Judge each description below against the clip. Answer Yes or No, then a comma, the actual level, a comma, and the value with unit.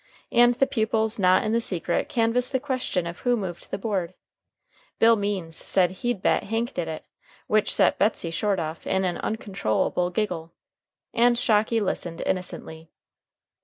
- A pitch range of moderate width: Yes, average, 4.4 semitones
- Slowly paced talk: No, average, 160 wpm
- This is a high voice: Yes, high, 205 Hz